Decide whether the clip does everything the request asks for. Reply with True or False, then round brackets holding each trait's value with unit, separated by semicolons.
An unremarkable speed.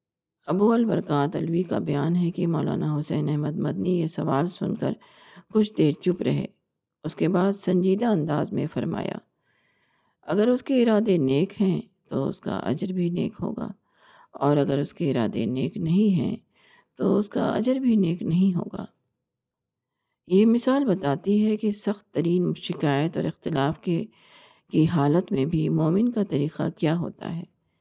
True (165 wpm)